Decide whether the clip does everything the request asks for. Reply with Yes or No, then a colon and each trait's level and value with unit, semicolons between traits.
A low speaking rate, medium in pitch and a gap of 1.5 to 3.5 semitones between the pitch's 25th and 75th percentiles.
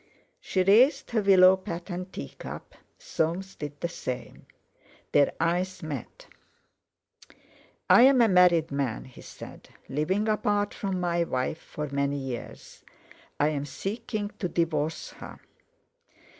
No: slow, 130 wpm; medium, 175 Hz; average, 5.0 semitones